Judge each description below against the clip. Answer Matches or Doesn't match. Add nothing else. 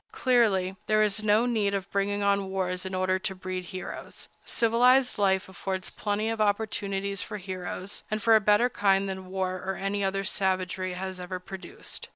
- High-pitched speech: Matches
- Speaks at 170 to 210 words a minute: Matches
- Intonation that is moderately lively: Doesn't match